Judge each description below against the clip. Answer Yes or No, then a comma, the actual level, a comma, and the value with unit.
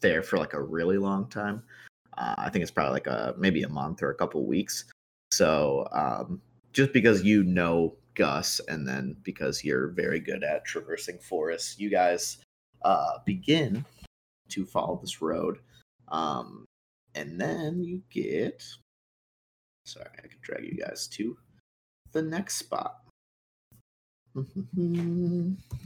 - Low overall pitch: Yes, low, 105 Hz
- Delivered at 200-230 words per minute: No, average, 140 wpm